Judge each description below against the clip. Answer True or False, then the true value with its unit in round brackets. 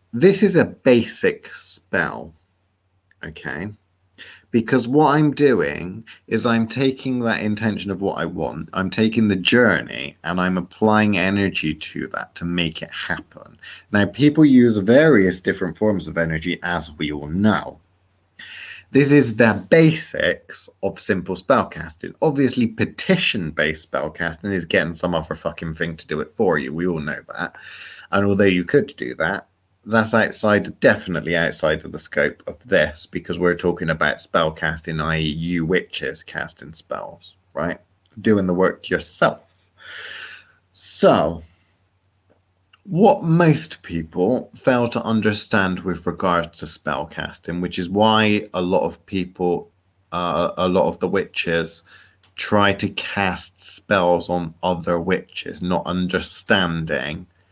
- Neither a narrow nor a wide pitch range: True (3.9 semitones)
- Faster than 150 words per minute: False (145 wpm)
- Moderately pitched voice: False (95 Hz)